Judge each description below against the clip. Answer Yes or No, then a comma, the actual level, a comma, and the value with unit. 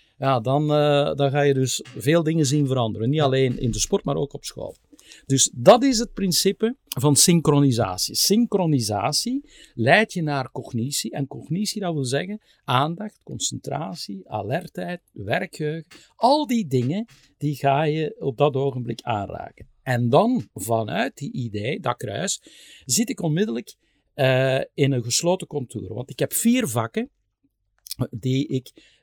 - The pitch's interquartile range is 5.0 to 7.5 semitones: Yes, wide, 5.6 semitones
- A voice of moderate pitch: Yes, medium, 145 Hz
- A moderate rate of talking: Yes, average, 150 wpm